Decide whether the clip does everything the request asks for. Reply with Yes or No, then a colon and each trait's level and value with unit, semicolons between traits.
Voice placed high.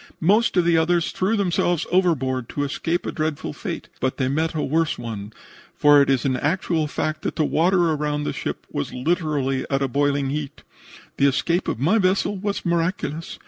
No: medium, 155 Hz